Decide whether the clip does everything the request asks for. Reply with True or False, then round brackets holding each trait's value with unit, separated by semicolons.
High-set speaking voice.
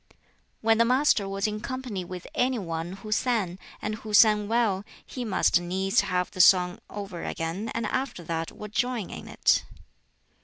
True (205 Hz)